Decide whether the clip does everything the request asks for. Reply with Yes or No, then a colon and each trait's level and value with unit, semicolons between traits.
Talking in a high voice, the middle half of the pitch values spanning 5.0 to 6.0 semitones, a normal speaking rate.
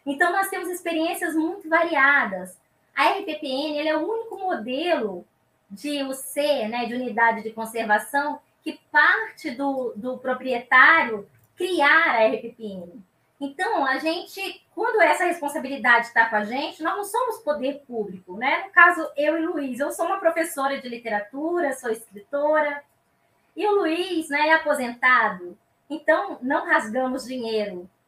Yes: very high, 285 Hz; wide, 5.6 semitones; average, 145 wpm